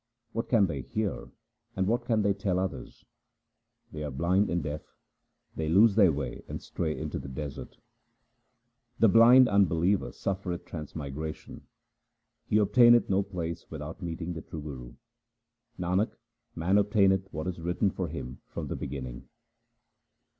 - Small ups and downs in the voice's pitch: No, average, 4.4 semitones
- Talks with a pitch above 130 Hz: No, very low, 90 Hz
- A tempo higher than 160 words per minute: No, average, 145 wpm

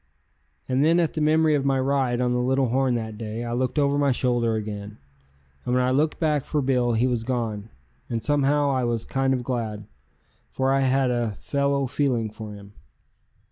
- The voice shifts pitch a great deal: No, average, 3.1 semitones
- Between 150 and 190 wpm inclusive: No, average, 200 wpm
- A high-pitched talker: No, low, 130 Hz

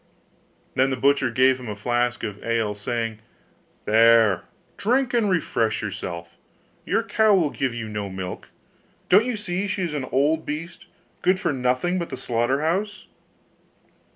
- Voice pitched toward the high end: No, low, 130 Hz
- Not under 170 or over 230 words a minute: No, average, 155 wpm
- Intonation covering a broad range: Yes, wide, 7.7 semitones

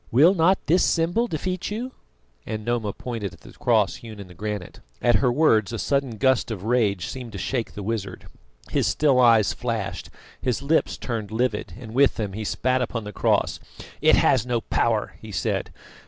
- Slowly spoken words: No, average, 190 wpm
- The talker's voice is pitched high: No, low, 115 Hz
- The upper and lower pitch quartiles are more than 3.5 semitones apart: Yes, average, 3.9 semitones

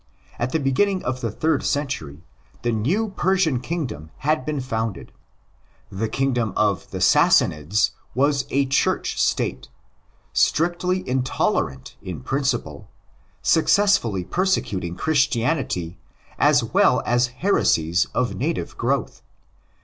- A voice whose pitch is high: No, low, 130 Hz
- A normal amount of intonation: No, wide, 6.6 semitones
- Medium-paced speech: No, slow, 115 wpm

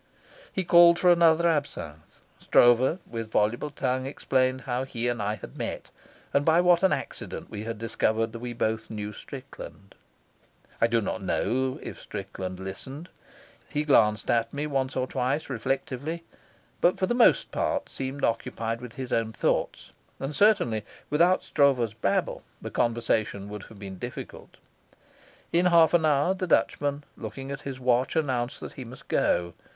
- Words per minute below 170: Yes, average, 160 wpm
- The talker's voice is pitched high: No, low, 130 Hz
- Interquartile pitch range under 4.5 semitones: No, average, 4.8 semitones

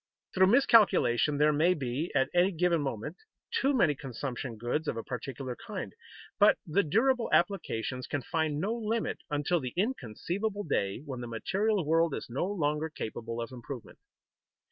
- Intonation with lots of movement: Yes, wide, 6.8 semitones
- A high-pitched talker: No, medium, 150 Hz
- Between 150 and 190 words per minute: Yes, average, 160 wpm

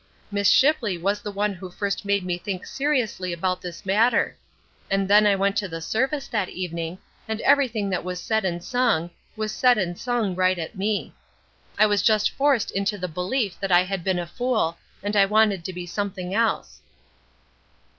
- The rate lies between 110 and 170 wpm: No, average, 190 wpm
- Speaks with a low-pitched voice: No, high, 200 Hz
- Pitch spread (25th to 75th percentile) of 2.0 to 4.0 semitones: Yes, average, 3.1 semitones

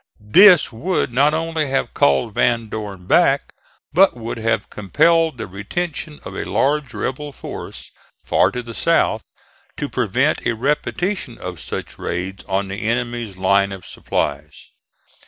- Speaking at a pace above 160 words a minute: No, average, 145 wpm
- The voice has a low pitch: Yes, low, 120 Hz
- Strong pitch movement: Yes, wide, 7.0 semitones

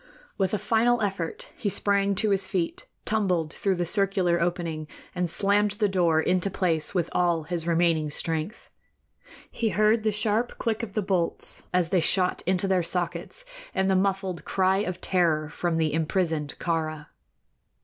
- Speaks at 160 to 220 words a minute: Yes, average, 165 wpm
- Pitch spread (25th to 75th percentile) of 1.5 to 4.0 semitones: Yes, average, 3.1 semitones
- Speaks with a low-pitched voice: No, medium, 185 Hz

